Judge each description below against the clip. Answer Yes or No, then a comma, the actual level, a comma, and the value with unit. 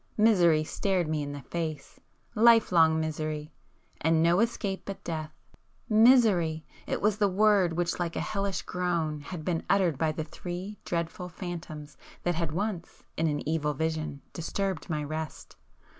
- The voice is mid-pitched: Yes, medium, 170 Hz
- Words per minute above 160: No, average, 145 wpm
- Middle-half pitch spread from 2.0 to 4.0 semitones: Yes, average, 3.7 semitones